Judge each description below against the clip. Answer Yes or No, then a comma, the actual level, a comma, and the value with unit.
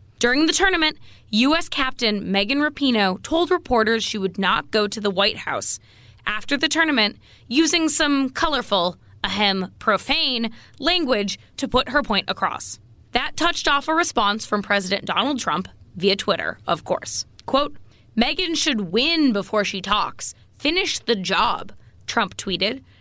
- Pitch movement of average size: No, wide, 6.8 semitones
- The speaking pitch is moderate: No, high, 230 Hz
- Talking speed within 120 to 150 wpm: Yes, average, 145 wpm